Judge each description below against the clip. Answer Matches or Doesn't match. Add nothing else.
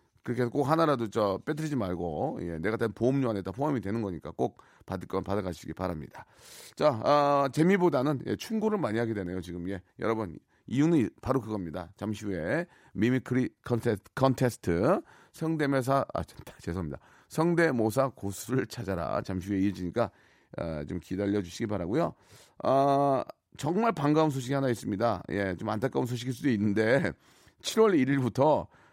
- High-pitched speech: Doesn't match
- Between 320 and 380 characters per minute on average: Matches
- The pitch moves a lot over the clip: Matches